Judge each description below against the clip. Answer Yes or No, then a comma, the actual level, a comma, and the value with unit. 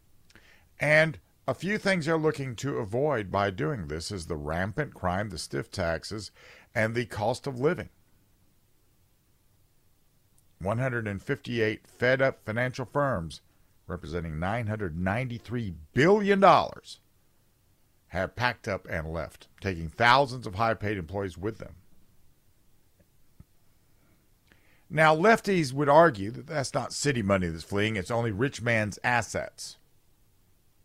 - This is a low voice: Yes, low, 105 Hz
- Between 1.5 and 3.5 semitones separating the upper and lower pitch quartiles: No, average, 4.9 semitones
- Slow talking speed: Yes, slow, 115 wpm